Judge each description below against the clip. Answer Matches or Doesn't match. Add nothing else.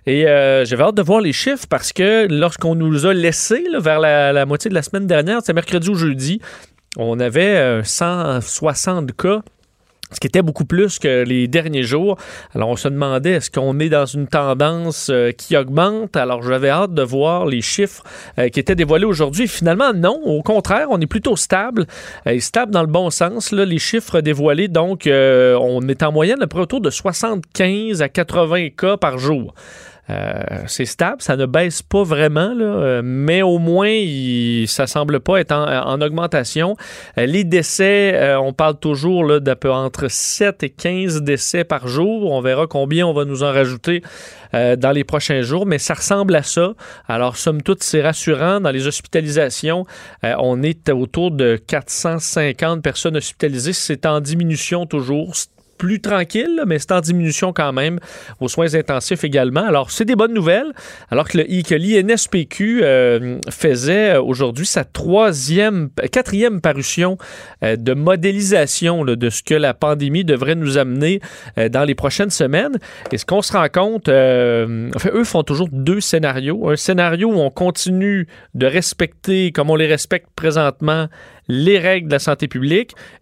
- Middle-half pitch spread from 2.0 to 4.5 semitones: Doesn't match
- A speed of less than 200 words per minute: Matches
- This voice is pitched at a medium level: Matches